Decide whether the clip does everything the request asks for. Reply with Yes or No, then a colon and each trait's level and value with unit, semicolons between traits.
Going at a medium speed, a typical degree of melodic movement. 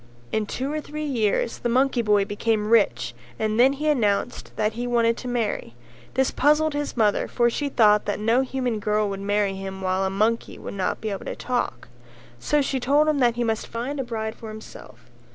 No: fast, 210 wpm; average, 3.9 semitones